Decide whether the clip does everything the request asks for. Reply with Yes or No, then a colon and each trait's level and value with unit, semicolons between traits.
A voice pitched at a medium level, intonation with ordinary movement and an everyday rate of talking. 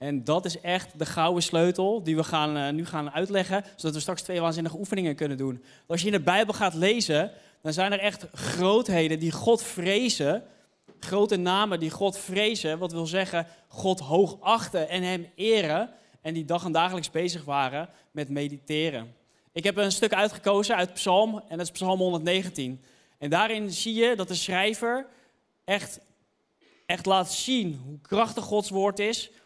Yes: medium, 180 Hz; average, 4.0 semitones; average, 175 wpm